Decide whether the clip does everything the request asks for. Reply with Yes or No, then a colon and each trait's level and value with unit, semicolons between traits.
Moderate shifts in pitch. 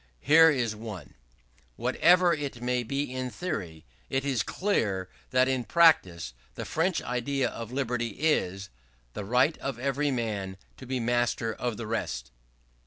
Yes: average, 4.5 semitones